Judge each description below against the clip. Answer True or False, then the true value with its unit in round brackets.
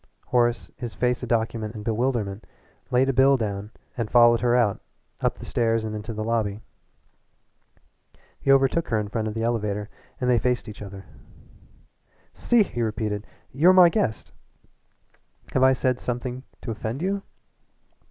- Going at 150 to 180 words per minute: True (160 wpm)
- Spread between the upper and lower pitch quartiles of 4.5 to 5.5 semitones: False (2.9 semitones)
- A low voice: True (120 Hz)